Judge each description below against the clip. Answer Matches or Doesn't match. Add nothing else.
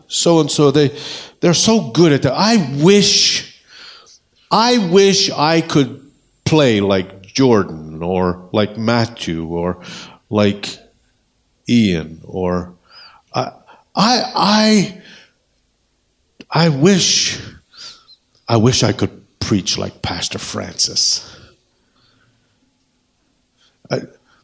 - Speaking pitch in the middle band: Matches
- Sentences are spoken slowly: Matches